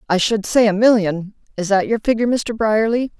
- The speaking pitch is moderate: No, high, 215 Hz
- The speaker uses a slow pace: No, fast, 205 wpm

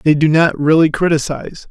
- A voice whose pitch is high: No, medium, 155 Hz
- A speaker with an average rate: Yes, average, 175 wpm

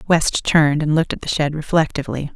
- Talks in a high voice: No, medium, 155 Hz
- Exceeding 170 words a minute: Yes, fast, 205 wpm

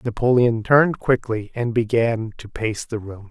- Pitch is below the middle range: Yes, low, 115 Hz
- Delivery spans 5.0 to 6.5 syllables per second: No, 4.5 syllables/s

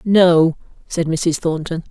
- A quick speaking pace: No, slow, 125 wpm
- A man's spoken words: No, female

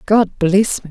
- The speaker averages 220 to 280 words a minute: No, average, 200 wpm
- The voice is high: Yes, high, 195 Hz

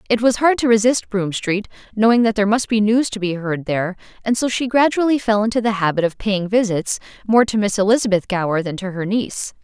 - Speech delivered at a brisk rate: Yes, fast, 230 wpm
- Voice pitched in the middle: No, high, 210 Hz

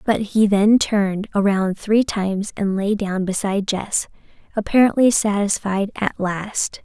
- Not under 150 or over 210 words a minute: No, average, 140 wpm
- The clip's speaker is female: Yes, female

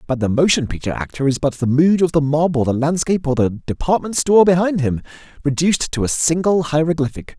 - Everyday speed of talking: No, fast, 210 wpm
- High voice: No, medium, 150 Hz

